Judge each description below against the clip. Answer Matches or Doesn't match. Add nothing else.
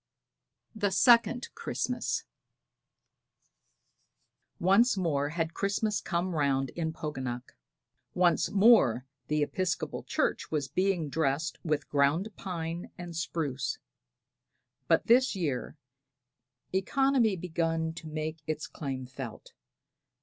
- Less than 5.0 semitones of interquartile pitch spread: Matches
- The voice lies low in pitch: Doesn't match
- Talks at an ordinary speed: Doesn't match